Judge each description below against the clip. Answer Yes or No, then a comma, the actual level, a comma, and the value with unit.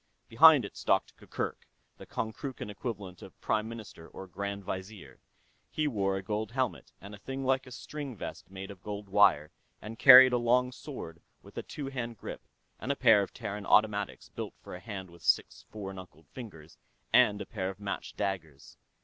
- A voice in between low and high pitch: No, low, 105 Hz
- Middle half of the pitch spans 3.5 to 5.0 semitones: Yes, average, 4.0 semitones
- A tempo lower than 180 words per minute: No, average, 185 wpm